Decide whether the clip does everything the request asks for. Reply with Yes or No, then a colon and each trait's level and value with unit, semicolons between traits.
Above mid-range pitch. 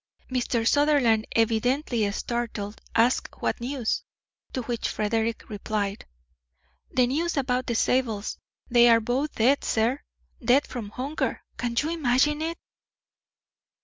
Yes: high, 245 Hz